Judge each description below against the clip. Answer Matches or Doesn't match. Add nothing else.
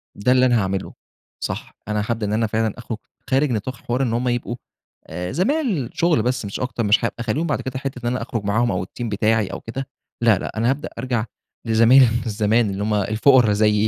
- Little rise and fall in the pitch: Doesn't match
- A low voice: Matches